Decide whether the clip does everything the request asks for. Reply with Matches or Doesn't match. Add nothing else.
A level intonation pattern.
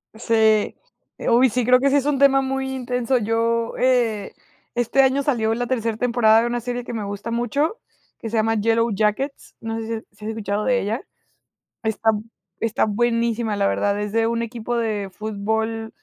Matches